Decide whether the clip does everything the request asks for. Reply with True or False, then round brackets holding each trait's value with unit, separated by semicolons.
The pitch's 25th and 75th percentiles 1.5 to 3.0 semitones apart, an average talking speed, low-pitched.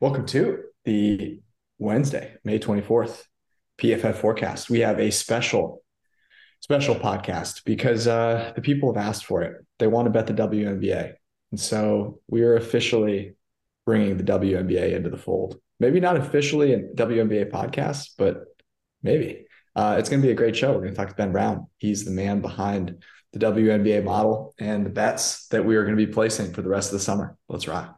True (2.5 semitones; 185 wpm; 110 Hz)